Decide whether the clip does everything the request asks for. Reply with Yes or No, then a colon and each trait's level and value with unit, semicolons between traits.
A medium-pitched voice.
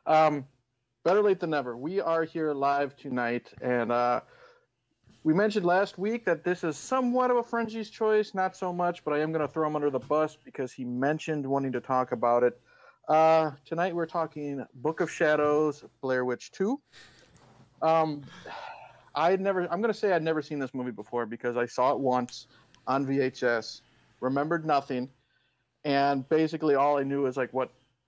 Yes: medium, 150 Hz